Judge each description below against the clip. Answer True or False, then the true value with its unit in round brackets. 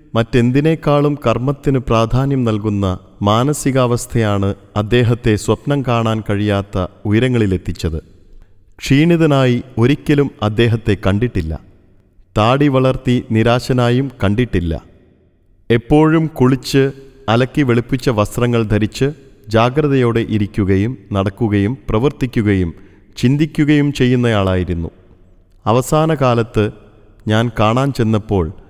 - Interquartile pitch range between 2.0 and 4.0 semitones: False (4.7 semitones)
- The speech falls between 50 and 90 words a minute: True (75 wpm)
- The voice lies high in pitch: False (115 Hz)